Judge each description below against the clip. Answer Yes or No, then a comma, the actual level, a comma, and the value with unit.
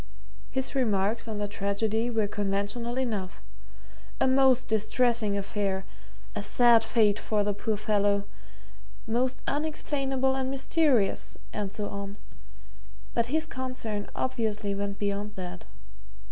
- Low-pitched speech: No, high, 220 Hz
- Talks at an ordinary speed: No, slow, 120 wpm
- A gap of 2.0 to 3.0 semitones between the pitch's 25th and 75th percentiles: No, average, 3.9 semitones